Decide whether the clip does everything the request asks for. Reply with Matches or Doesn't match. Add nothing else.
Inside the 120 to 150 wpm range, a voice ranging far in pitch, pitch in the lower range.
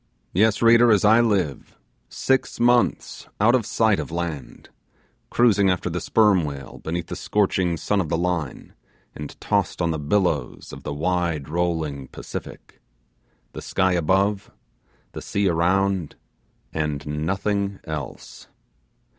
Doesn't match